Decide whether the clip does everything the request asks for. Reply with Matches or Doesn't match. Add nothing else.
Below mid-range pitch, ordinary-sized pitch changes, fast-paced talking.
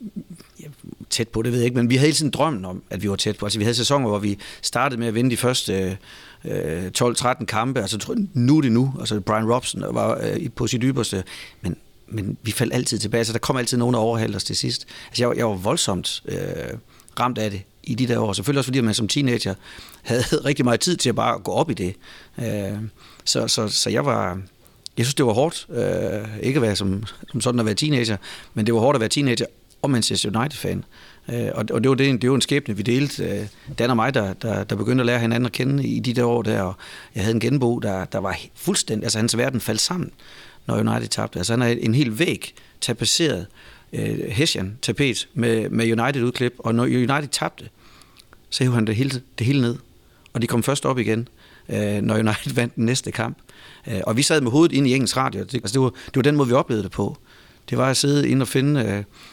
Matches